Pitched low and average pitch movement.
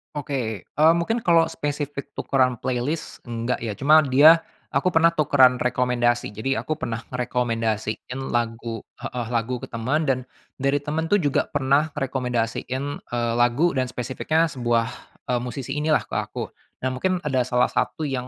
Yes: low, 130 Hz; average, 3.6 semitones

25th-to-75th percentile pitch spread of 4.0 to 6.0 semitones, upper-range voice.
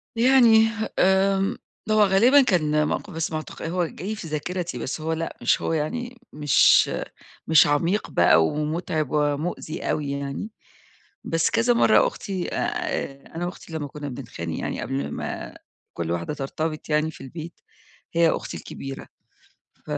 No: average, 4.6 semitones; medium, 160 Hz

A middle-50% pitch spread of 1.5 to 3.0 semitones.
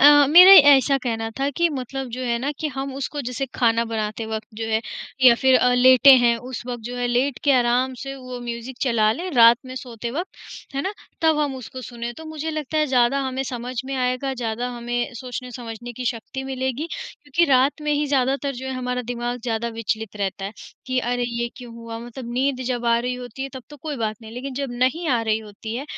Yes: narrow, 2.5 semitones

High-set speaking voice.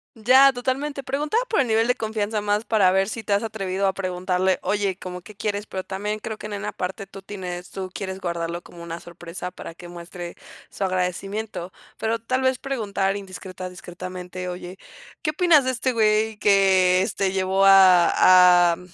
Yes: high, 195 Hz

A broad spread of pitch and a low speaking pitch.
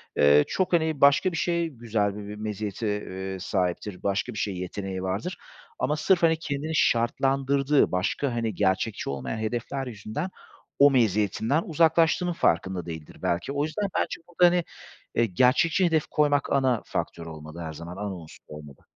Yes: wide, 8.1 semitones; low, 115 Hz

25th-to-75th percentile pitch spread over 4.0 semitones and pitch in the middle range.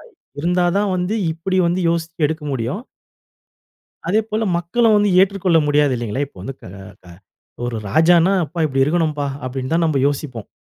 Yes: average, 4.5 semitones; medium, 165 Hz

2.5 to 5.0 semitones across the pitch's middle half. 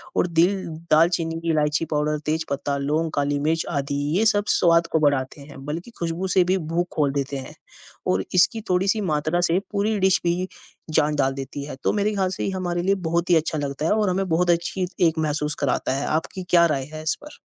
Yes: average, 3.6 semitones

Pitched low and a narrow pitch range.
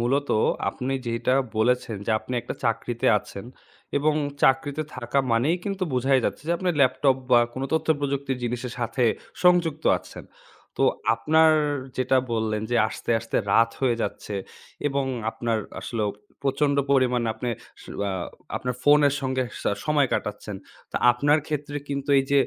No: low, 130 Hz; average, 3.4 semitones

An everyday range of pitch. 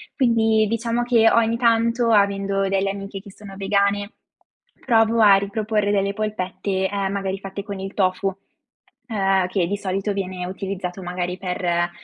No: narrow, 2.1 semitones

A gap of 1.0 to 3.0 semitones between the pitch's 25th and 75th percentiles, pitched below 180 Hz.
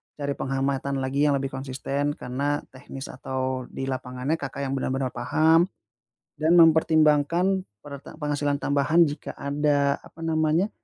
Yes: narrow, 2.6 semitones; medium, 140 Hz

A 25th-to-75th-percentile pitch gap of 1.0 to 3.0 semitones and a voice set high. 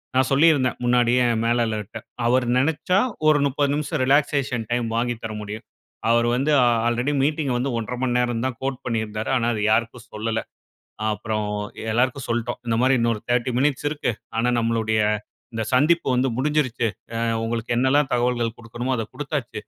No: narrow, 2.5 semitones; low, 120 Hz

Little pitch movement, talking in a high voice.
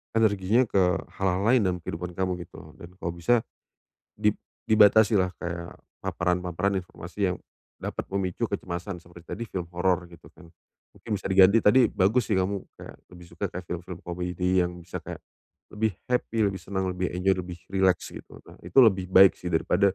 No: narrow, 2.1 semitones; very low, 95 Hz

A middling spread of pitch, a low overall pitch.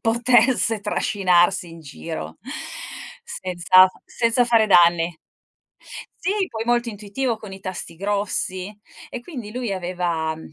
No: average, 4.9 semitones; high, 200 Hz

